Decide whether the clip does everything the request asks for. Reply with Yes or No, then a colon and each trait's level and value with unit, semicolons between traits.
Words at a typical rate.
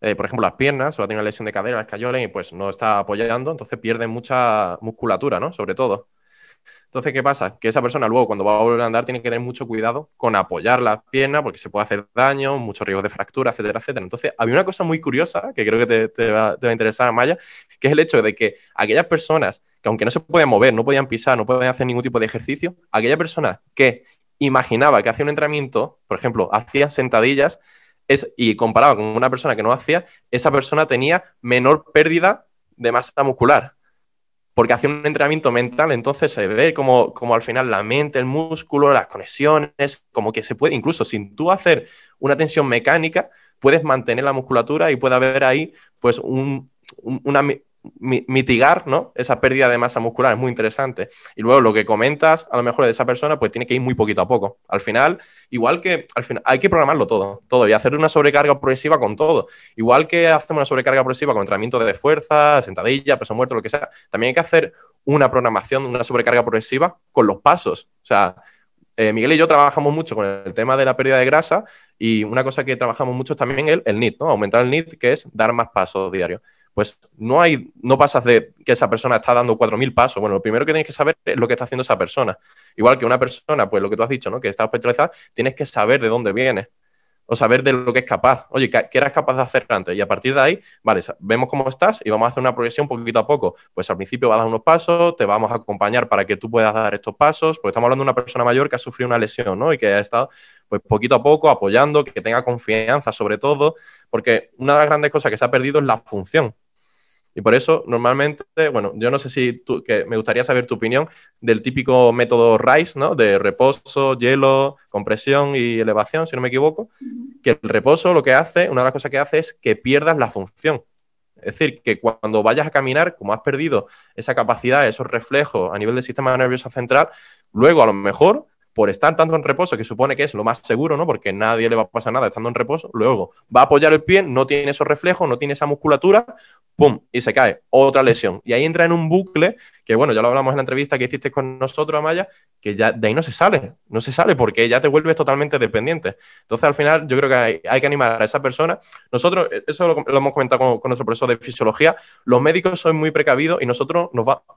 No: fast, 235 wpm